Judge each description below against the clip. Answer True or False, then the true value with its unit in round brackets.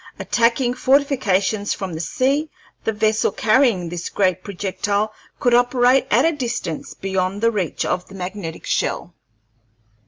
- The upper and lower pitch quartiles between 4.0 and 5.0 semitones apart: True (4.7 semitones)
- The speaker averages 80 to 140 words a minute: True (135 wpm)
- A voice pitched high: True (215 Hz)